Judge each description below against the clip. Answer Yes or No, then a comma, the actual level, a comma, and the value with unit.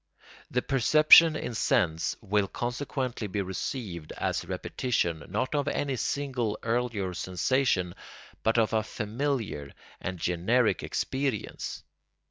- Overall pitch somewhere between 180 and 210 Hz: No, low, 115 Hz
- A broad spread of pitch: Yes, wide, 5.8 semitones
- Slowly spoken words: Yes, slow, 115 wpm